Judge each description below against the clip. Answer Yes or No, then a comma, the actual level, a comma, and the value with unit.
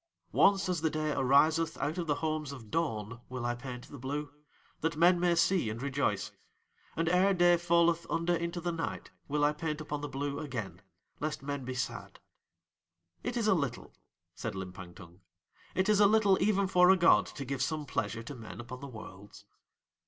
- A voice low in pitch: No, medium, 150 Hz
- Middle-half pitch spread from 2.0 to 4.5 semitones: No, average, 5.3 semitones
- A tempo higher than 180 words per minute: Yes, average, 195 wpm